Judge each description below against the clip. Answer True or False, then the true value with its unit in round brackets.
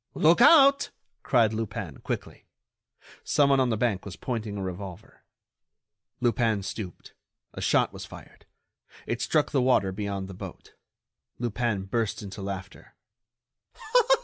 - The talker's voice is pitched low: True (110 Hz)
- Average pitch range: True (4.1 semitones)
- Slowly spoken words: True (125 wpm)